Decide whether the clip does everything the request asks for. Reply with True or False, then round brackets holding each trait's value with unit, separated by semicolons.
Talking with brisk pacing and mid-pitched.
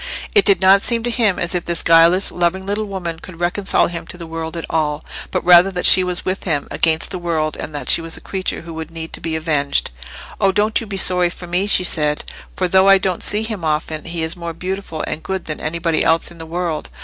True (245 wpm; 175 Hz)